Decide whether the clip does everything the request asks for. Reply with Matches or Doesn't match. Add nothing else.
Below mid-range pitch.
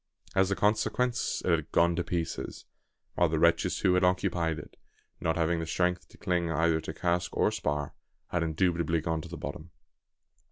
Matches